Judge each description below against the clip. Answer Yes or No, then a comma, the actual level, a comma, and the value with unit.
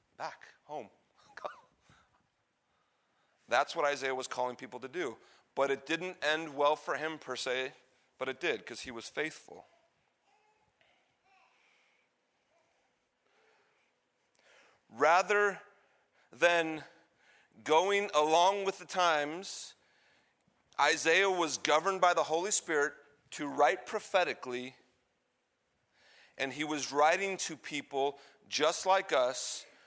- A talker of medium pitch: Yes, medium, 160 Hz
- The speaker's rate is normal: No, slow, 105 wpm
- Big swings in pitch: Yes, wide, 6.0 semitones